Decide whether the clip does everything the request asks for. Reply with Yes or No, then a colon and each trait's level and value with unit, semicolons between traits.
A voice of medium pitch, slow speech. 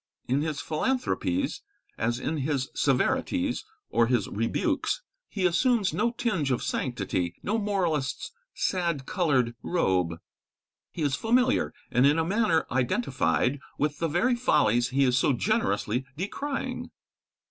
Yes: medium, 155 Hz; slow, 130 wpm